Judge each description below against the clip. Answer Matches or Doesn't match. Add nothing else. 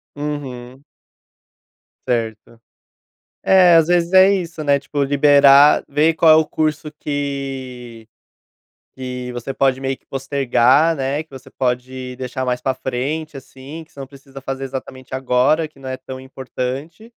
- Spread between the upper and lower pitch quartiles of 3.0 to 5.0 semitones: Doesn't match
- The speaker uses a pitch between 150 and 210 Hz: Doesn't match